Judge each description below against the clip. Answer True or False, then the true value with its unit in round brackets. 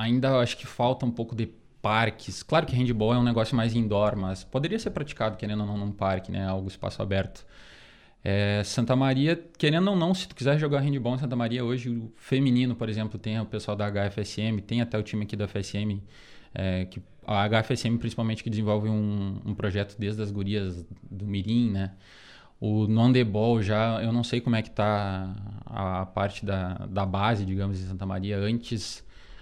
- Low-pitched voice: True (110 Hz)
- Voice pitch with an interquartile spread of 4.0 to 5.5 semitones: False (3.1 semitones)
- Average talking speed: False (200 wpm)